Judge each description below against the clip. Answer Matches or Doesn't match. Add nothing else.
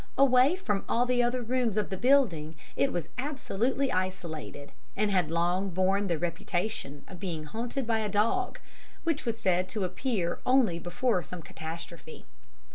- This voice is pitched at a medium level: Doesn't match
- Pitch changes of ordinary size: Doesn't match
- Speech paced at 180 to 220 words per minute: Doesn't match